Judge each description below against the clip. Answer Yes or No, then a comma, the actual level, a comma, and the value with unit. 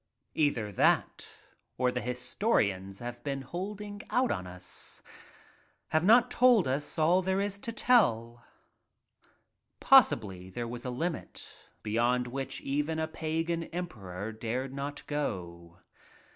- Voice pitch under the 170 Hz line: Yes, low, 135 Hz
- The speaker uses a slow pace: Yes, slow, 125 wpm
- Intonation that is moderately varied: No, wide, 7.2 semitones